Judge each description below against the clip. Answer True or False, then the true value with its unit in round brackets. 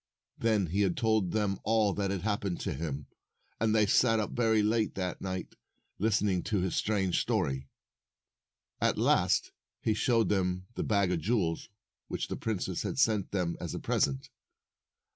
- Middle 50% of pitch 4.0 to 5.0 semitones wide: False (3.2 semitones)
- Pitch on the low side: True (100 Hz)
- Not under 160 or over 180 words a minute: True (165 wpm)